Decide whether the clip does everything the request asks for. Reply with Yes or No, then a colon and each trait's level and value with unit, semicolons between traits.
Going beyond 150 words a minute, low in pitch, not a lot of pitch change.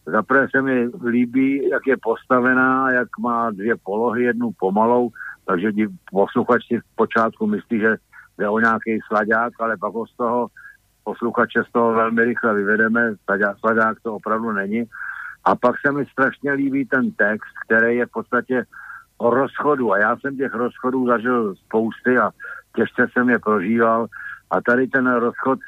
Yes: average, 160 wpm; low, 120 Hz; narrow, 2.3 semitones